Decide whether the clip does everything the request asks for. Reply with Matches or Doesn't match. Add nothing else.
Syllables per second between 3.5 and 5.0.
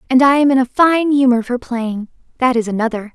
Doesn't match